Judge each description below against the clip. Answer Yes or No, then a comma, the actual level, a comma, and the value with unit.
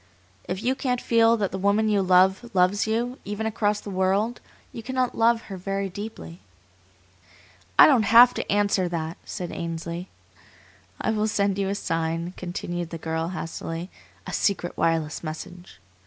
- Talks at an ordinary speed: Yes, average, 160 wpm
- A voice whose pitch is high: Yes, high, 195 Hz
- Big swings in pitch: No, average, 4.0 semitones